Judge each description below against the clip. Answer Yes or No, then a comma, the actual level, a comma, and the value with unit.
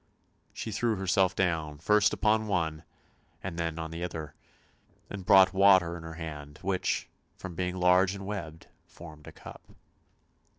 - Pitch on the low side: Yes, very low, 90 Hz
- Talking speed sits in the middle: Yes, average, 155 wpm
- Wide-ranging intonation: No, average, 3.1 semitones